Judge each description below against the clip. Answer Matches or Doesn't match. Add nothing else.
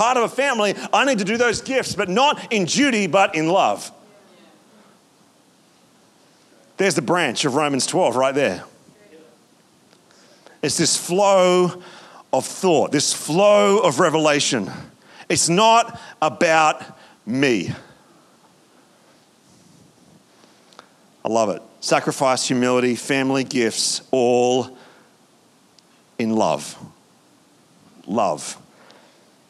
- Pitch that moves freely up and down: Matches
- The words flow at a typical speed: Doesn't match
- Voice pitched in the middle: Matches